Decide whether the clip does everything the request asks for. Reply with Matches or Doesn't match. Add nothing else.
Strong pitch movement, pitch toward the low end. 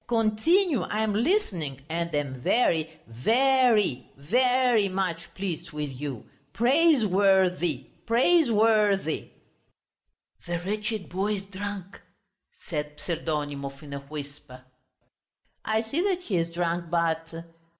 Doesn't match